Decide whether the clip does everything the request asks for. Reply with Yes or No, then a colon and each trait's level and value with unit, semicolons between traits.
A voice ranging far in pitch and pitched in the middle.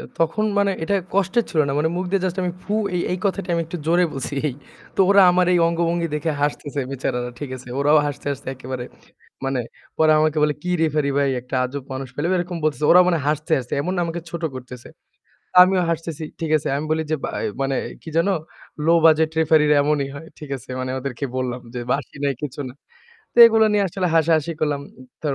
No: average, 3.6 semitones; medium, 155 Hz